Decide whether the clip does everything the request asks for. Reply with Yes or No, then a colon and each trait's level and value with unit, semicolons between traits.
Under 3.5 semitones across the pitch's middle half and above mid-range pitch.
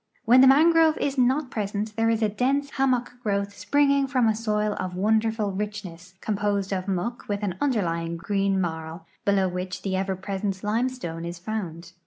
No: average, 4.3 semitones; high, 210 Hz